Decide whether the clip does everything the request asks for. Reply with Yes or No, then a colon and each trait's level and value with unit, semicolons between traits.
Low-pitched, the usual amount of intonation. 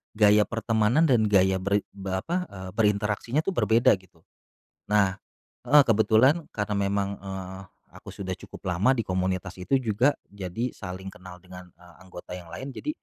Yes: low, 100 Hz; average, 3.5 semitones